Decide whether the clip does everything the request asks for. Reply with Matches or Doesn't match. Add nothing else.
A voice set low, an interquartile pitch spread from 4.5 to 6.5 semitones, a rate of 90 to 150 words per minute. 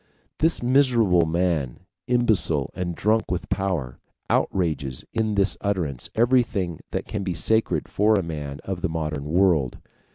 Matches